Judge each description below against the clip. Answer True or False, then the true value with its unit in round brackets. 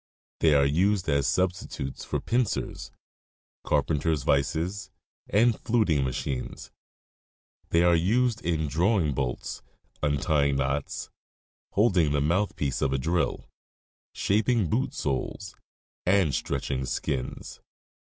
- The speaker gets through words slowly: True (110 wpm)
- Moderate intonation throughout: False (5.8 semitones)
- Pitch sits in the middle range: False (80 Hz)